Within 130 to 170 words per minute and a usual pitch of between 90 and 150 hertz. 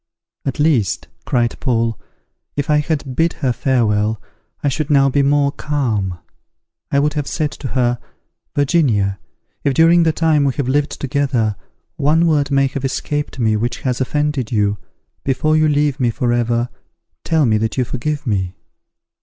Yes: average, 160 wpm; low, 135 Hz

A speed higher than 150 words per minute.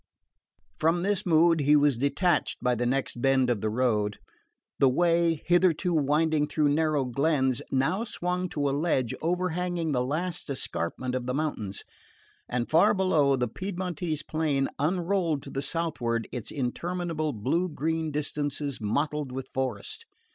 No: average, 145 wpm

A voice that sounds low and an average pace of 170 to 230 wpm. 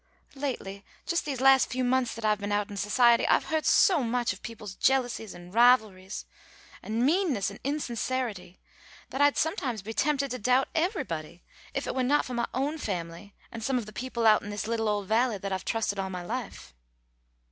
No: high, 235 Hz; average, 200 wpm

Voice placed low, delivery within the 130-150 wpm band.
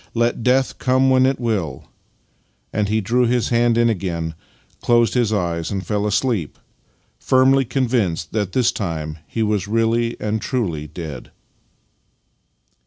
Yes: low, 110 Hz; average, 140 wpm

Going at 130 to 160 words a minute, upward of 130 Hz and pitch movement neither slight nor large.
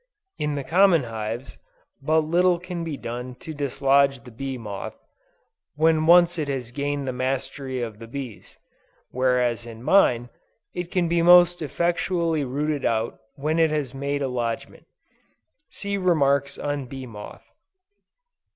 Yes: average, 145 wpm; medium, 140 Hz; average, 4.6 semitones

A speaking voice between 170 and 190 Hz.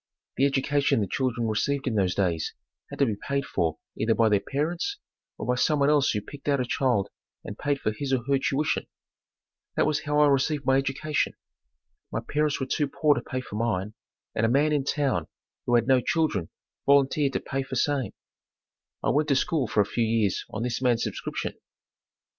No: low, 135 Hz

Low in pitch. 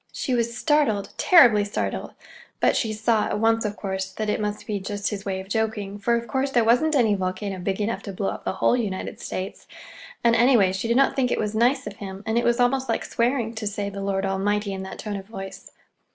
No: high, 215 Hz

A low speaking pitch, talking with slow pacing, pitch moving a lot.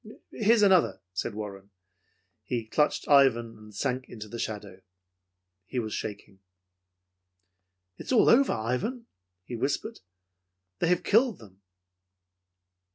Yes: low, 120 Hz; slow, 120 wpm; wide, 8.7 semitones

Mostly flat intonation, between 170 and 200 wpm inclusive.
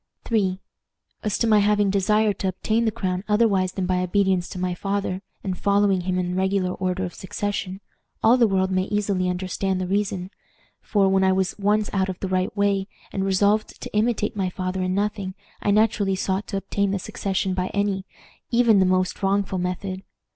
Yes: narrow, 1.7 semitones; average, 190 wpm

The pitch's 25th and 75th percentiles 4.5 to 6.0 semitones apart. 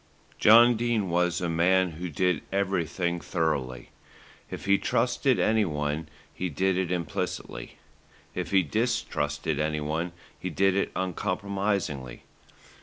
No: average, 4.0 semitones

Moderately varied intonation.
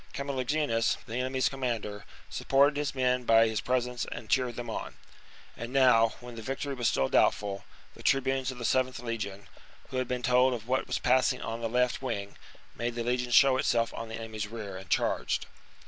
No: narrow, 2.3 semitones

